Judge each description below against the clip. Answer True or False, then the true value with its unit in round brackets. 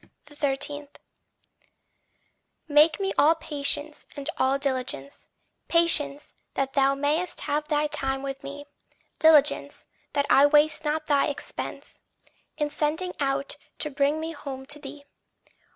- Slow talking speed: True (125 wpm)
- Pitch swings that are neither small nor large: False (1.7 semitones)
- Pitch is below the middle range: False (290 Hz)